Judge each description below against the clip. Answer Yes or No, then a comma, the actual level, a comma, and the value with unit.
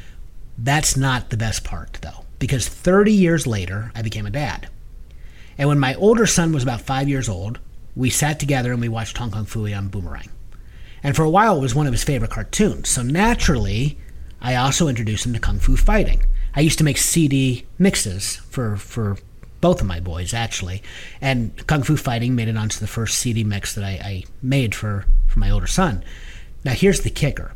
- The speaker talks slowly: No, average, 200 wpm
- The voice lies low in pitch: Yes, low, 115 Hz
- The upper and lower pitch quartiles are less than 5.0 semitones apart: No, wide, 5.6 semitones